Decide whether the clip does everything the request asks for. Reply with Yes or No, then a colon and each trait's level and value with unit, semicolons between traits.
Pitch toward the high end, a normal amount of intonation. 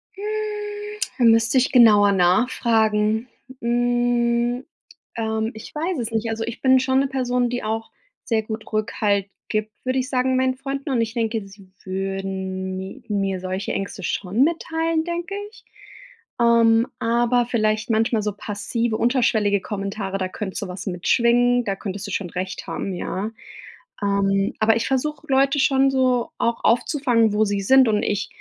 Yes: high, 225 Hz; average, 3.7 semitones